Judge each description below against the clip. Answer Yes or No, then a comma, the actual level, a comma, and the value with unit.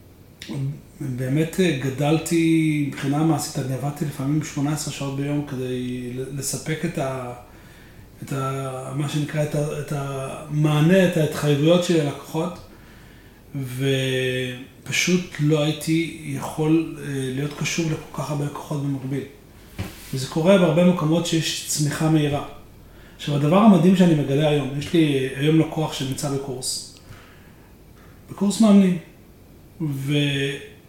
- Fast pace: No, average, 115 wpm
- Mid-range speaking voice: Yes, medium, 145 Hz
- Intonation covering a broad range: No, average, 2.9 semitones